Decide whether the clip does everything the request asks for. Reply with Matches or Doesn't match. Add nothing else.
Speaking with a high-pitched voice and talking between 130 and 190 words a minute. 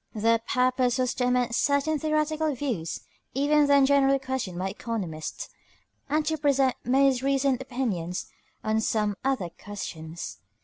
Matches